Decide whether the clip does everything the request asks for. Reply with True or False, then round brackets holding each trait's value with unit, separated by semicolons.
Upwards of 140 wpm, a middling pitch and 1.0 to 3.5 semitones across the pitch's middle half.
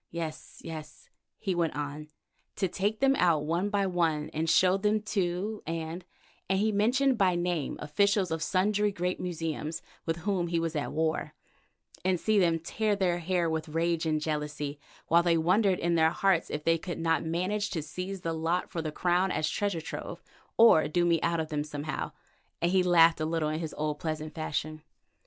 True (195 wpm; 170 Hz; 3.0 semitones)